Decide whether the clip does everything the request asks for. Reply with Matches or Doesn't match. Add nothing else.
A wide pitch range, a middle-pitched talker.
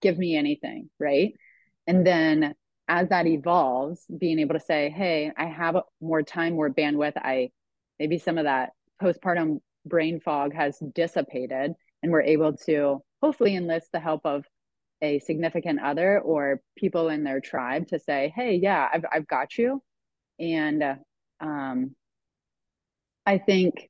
Doesn't match